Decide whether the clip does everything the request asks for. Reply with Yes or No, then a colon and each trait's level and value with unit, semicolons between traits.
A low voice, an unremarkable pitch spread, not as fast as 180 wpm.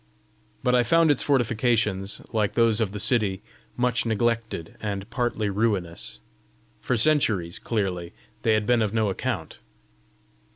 Yes: low, 110 Hz; average, 3.2 semitones; slow, 135 wpm